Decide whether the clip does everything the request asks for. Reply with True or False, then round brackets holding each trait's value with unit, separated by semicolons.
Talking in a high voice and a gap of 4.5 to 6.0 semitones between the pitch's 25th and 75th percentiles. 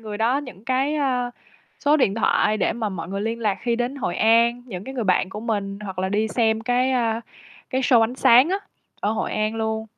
False (225 Hz; 3.0 semitones)